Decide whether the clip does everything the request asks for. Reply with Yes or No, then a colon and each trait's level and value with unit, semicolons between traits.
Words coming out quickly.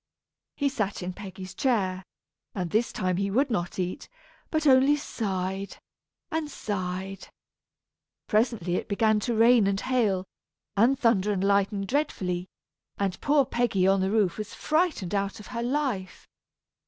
No: average, 145 wpm